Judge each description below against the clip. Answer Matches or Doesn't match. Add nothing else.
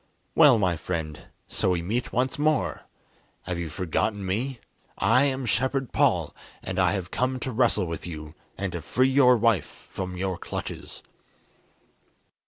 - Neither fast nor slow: Matches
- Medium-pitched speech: Doesn't match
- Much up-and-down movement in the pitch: Matches